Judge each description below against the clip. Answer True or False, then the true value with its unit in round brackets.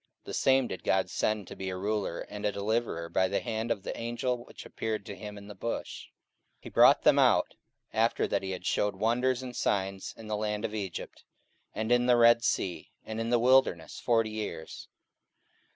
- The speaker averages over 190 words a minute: True (205 wpm)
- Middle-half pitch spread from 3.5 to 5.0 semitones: False (3.0 semitones)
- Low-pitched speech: True (110 Hz)